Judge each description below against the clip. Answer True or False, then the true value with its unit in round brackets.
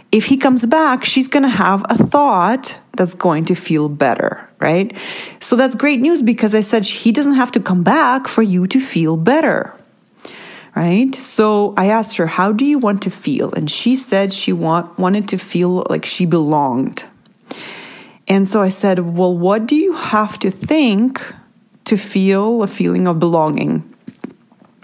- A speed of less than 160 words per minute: False (175 wpm)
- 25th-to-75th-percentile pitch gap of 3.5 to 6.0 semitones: True (5.5 semitones)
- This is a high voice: True (210 Hz)